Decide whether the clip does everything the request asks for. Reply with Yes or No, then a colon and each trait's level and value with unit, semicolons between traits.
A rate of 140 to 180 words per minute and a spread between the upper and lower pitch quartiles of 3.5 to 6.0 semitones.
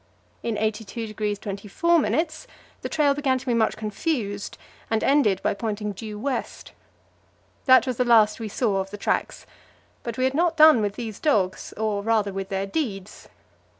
Yes: average, 165 wpm; average, 4.1 semitones